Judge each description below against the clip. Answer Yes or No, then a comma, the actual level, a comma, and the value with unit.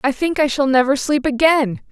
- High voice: Yes, very high, 280 Hz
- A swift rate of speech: Yes, fast, 220 wpm